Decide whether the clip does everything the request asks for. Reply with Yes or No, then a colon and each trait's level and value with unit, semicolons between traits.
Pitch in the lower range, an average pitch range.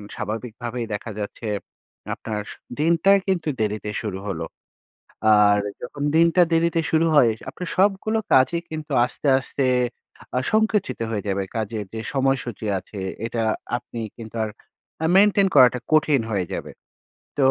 No: low, 125 Hz; wide, 7.1 semitones